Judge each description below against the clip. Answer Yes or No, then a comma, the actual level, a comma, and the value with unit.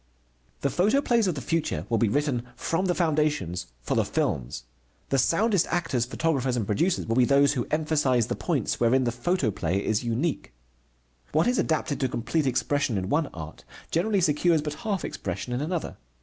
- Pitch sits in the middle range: Yes, medium, 145 Hz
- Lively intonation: Yes, wide, 5.7 semitones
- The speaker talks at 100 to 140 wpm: No, average, 180 wpm